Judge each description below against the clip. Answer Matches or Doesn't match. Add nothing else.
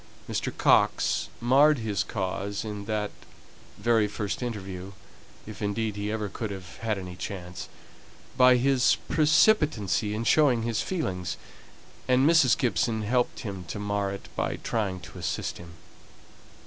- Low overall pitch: Matches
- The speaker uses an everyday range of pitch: Matches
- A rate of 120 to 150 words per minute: Matches